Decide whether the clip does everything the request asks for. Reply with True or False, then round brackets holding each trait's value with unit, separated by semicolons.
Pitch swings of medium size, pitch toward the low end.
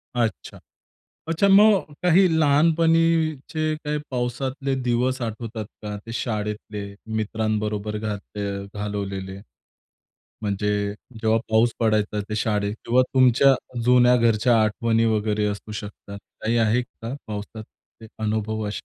True (3.5 semitones; 110 Hz)